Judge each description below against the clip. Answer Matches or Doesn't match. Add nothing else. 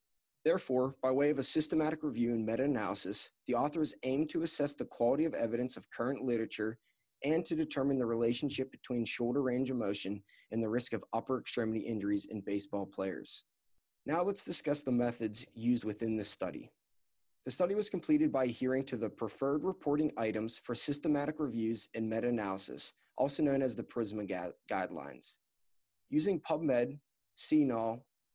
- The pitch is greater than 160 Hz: Doesn't match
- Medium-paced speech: Matches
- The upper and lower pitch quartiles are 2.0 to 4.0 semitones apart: Doesn't match